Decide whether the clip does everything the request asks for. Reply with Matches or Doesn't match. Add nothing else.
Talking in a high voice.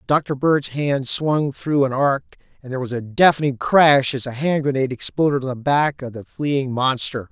Doesn't match